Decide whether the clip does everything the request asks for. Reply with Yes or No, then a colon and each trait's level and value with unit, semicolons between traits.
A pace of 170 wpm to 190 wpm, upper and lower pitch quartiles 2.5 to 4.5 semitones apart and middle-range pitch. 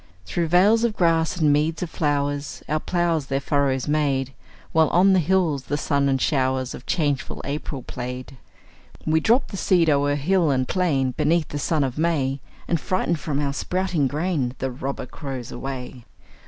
Yes: average, 175 wpm; average, 3.8 semitones; medium, 145 Hz